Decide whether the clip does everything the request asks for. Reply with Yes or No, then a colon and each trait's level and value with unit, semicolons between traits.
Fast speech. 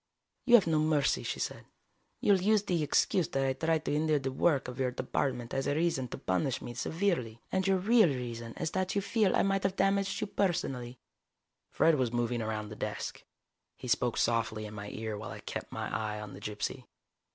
Yes: fast, 215 wpm